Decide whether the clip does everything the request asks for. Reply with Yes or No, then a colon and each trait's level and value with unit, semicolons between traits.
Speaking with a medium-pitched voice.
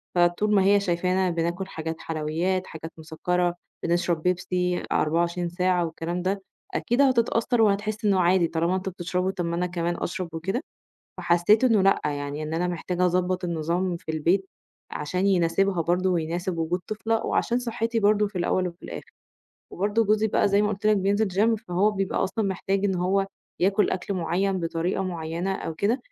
Yes: medium, 180 Hz